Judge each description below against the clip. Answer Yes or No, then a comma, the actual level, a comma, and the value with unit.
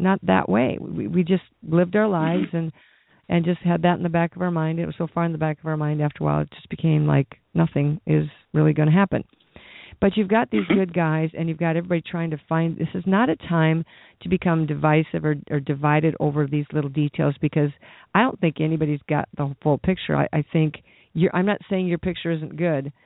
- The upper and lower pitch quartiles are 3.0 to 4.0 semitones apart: No, narrow, 2.6 semitones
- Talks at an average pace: No, fast, 240 wpm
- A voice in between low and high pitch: Yes, medium, 160 Hz